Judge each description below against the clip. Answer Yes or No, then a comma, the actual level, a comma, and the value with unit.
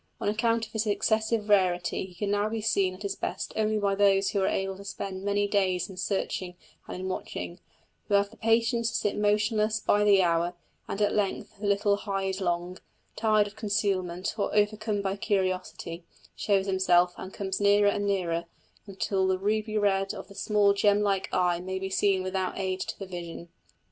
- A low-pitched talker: No, high, 200 Hz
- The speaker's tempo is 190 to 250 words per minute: Yes, average, 195 wpm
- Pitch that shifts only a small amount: Yes, narrow, 1.8 semitones